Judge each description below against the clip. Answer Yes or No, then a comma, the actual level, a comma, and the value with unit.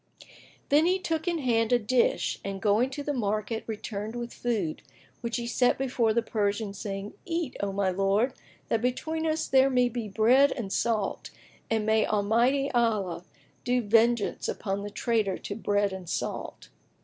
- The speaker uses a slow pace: No, average, 170 wpm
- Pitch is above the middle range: Yes, high, 230 Hz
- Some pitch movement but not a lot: Yes, average, 3.6 semitones